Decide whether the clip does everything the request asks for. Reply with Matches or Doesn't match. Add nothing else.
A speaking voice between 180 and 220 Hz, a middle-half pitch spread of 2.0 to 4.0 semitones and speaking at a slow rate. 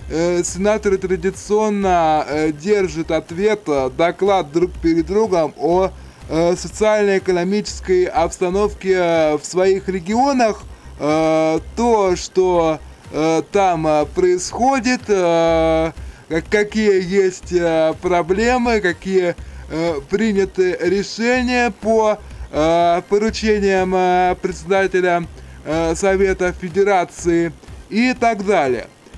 Matches